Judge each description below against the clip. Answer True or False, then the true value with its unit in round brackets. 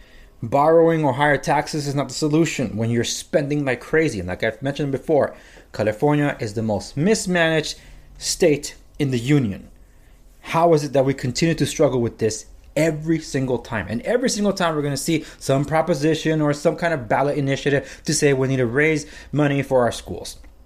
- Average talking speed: True (190 wpm)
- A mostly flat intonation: False (4.1 semitones)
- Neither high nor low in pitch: True (145 Hz)